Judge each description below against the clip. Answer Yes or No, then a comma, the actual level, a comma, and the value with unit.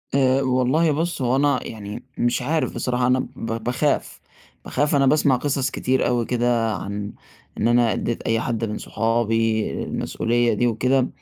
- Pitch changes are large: No, average, 2.8 semitones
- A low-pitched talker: Yes, low, 120 Hz